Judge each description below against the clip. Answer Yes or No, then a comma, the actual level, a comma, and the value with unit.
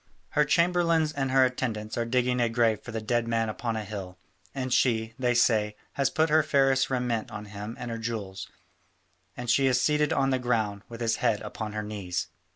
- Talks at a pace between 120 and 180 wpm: No, fast, 205 wpm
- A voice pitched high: No, low, 120 Hz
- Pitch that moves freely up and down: No, average, 3.5 semitones